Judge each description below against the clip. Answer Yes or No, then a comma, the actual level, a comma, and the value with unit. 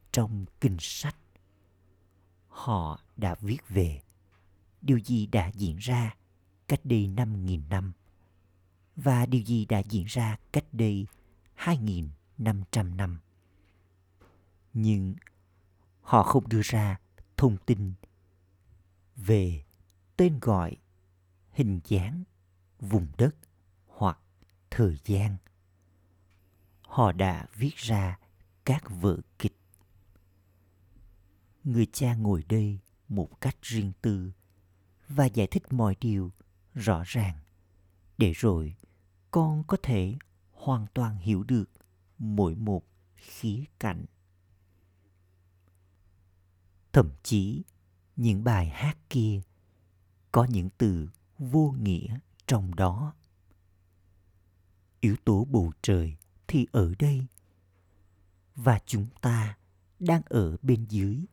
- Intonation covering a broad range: No, average, 3.3 semitones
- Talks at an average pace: No, slow, 105 wpm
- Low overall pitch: Yes, very low, 95 Hz